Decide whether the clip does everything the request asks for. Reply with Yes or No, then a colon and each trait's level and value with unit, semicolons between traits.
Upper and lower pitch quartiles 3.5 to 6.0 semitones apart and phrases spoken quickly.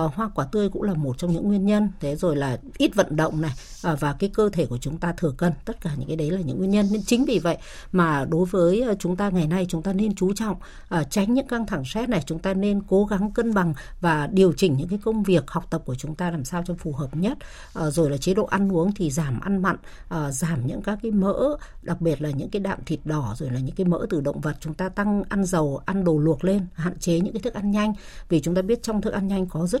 Yes: average, 4.3 semitones; fast, 280 wpm